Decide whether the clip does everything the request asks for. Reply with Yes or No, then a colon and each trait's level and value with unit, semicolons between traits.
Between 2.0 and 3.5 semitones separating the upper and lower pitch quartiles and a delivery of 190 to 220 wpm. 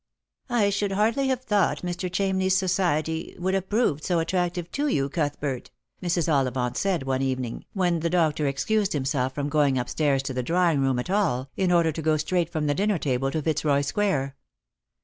No: average, 5.3 semitones; average, 195 wpm